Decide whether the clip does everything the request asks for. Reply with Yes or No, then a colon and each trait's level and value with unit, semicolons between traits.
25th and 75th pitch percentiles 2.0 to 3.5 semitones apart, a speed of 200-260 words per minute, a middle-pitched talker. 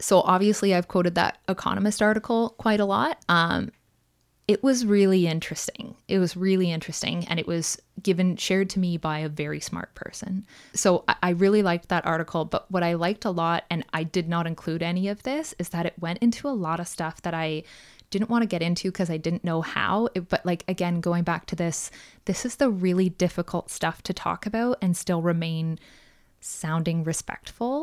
Yes: average, 2.8 semitones; fast, 205 wpm; medium, 180 Hz